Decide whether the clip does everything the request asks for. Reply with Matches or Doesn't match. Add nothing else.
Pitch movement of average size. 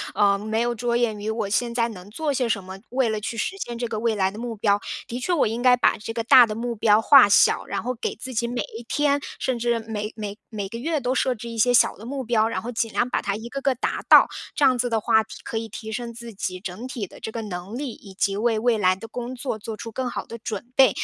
Doesn't match